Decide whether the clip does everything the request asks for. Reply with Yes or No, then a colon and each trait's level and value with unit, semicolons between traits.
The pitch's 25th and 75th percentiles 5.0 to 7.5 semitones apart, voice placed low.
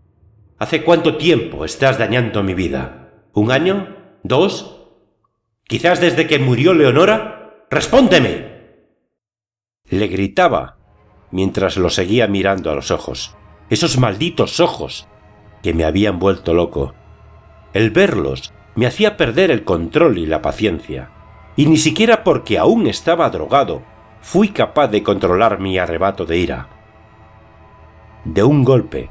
Yes: wide, 5.6 semitones; low, 105 Hz